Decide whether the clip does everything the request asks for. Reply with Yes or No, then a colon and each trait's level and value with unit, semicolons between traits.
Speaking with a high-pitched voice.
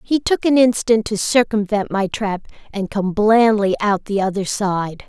Yes: high, 210 Hz